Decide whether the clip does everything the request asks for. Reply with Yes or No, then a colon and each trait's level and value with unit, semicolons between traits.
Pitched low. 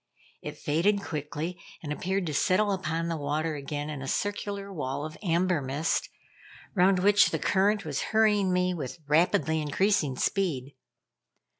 No: medium, 165 Hz